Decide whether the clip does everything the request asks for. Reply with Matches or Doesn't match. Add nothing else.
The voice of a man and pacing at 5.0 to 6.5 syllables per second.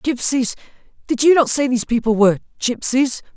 Matches